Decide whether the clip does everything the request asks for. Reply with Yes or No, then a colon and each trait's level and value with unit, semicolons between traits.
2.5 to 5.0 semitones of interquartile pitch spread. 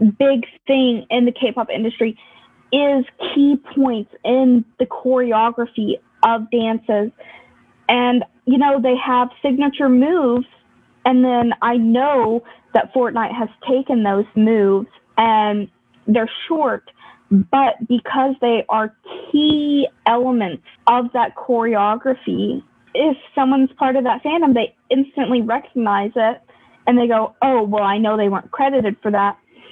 Yes: average, 3.1 semitones